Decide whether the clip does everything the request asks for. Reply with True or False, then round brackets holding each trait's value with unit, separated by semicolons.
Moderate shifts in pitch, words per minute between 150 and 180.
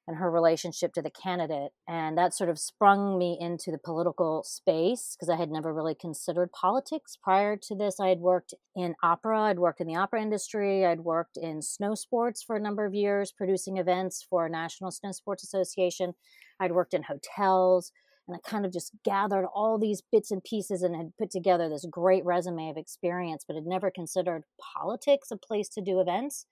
False (3.1 semitones; 200 wpm)